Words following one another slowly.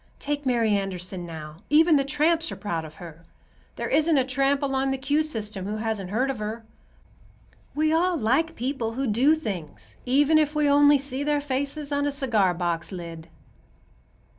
No: average, 180 wpm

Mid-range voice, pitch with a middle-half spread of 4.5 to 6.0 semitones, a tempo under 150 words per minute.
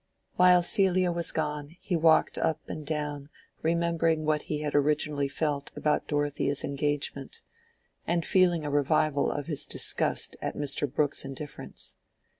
No: medium, 150 Hz; narrow, 2.4 semitones; average, 140 wpm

